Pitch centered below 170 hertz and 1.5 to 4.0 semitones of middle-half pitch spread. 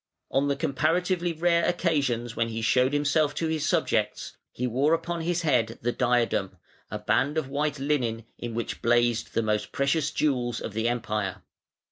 No: low, 135 Hz; average, 4.9 semitones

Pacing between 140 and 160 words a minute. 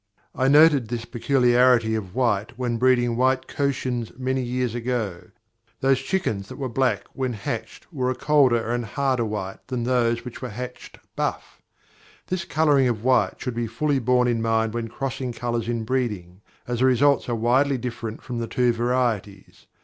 No: average, 170 wpm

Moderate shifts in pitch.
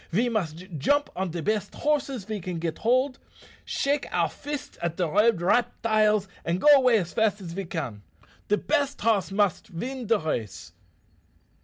No: wide, 6.4 semitones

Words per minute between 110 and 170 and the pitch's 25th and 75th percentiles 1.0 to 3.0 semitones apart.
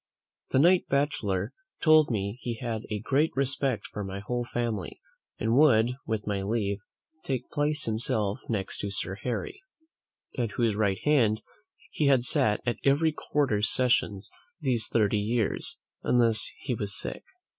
No: average, 145 wpm; average, 4.6 semitones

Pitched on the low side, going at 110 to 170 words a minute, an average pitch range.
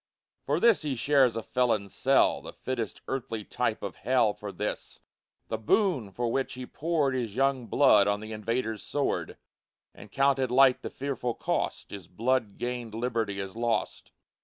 Yes: low, 120 Hz; average, 165 wpm; average, 3.7 semitones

